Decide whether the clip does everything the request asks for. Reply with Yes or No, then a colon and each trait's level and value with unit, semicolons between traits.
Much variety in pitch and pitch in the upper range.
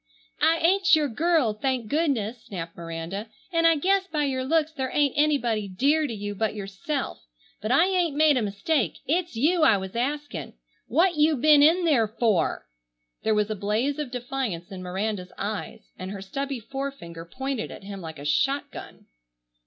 Yes: wide, 6.9 semitones; very high, 255 Hz